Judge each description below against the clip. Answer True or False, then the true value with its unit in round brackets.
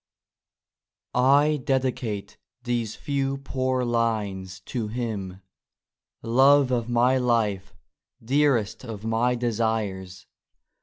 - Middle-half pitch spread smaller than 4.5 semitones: True (3.4 semitones)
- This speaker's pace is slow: True (100 wpm)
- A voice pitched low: True (120 Hz)